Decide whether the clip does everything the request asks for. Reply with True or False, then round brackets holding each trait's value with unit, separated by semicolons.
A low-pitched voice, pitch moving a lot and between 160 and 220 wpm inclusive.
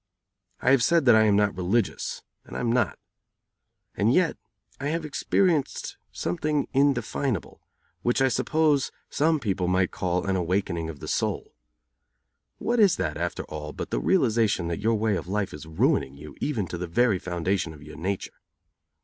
True (105 Hz; 7.2 semitones; 175 wpm)